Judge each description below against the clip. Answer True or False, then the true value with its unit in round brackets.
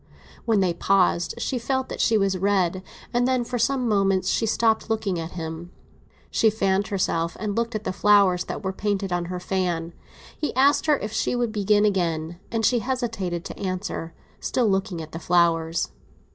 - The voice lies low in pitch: False (195 Hz)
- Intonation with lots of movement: False (4.1 semitones)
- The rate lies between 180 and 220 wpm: True (185 wpm)